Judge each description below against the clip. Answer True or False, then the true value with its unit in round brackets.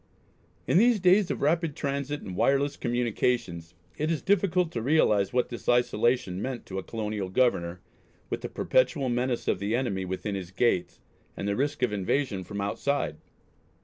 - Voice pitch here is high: False (120 Hz)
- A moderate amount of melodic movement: False (6.2 semitones)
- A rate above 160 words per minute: True (170 wpm)